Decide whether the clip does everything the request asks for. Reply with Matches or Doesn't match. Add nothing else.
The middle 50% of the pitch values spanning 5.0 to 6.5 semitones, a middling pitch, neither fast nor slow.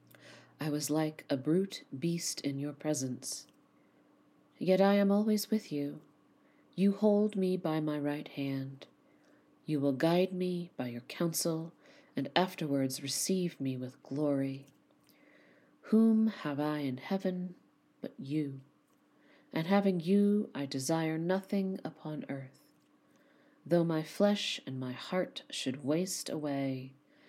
Doesn't match